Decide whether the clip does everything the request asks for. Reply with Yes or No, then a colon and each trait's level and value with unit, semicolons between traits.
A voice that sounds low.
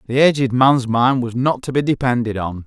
Yes: low, 125 Hz